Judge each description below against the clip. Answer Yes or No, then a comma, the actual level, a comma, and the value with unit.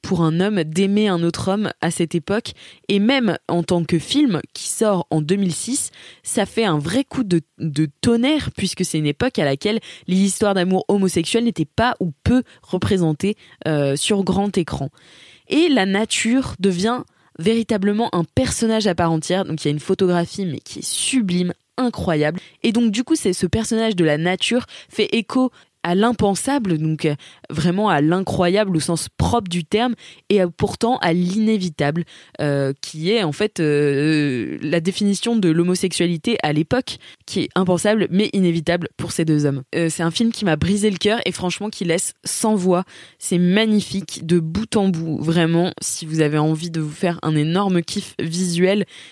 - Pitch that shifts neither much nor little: Yes, average, 4.3 semitones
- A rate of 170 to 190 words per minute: Yes, average, 185 wpm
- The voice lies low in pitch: No, medium, 180 Hz